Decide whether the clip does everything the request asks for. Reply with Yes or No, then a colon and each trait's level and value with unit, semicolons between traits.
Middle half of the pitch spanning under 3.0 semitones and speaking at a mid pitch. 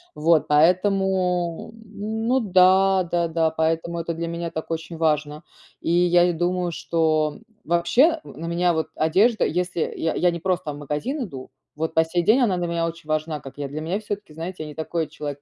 Yes: narrow, 2.6 semitones; medium, 170 Hz